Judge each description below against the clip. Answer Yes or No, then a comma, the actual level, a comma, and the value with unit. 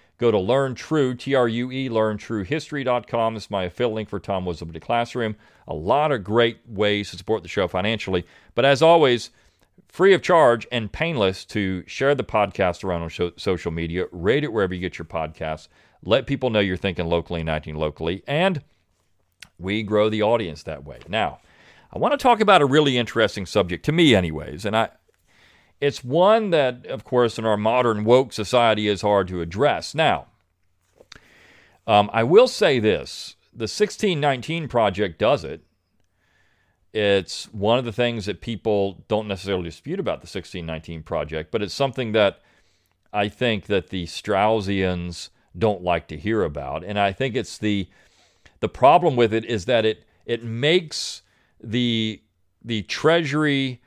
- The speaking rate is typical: Yes, average, 165 wpm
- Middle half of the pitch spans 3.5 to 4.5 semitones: No, average, 5.2 semitones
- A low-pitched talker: Yes, low, 105 Hz